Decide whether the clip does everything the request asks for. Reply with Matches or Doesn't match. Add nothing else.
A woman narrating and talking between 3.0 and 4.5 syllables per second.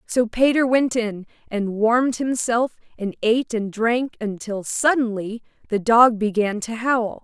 Matches